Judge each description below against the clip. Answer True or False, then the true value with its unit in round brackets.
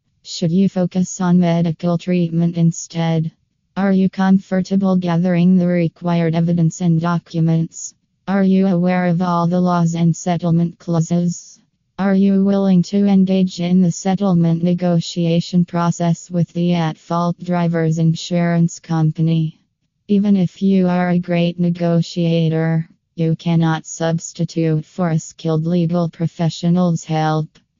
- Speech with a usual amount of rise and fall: False (1.6 semitones)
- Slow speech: True (125 wpm)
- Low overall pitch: False (170 Hz)